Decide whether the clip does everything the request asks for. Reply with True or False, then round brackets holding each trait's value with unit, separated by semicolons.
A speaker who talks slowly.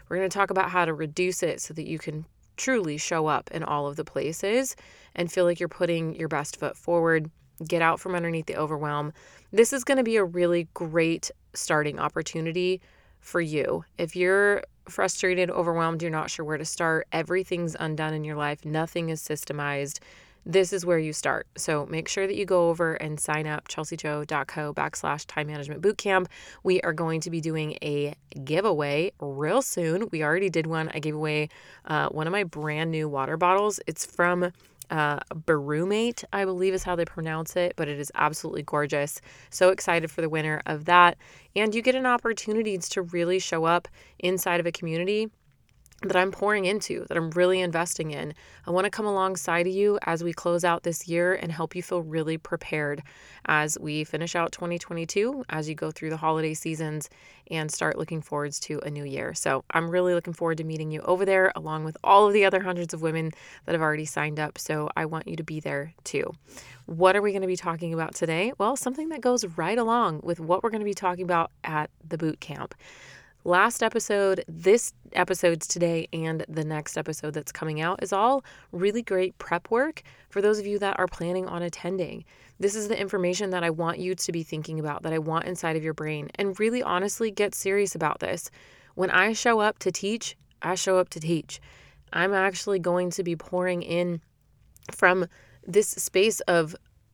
False (205 wpm)